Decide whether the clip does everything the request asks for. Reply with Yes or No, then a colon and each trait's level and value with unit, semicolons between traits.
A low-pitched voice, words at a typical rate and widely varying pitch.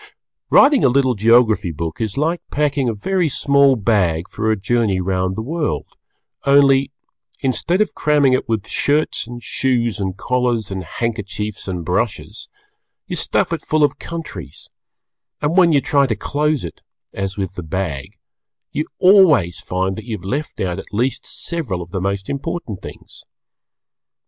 Yes: low, 115 Hz; average, 165 wpm; wide, 6.8 semitones